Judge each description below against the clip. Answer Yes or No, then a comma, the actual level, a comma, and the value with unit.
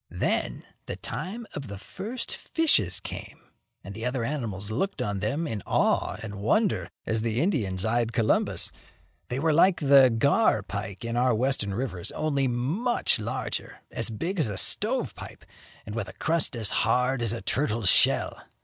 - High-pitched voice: No, low, 120 Hz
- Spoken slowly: No, average, 170 wpm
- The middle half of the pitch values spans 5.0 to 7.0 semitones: Yes, wide, 5.6 semitones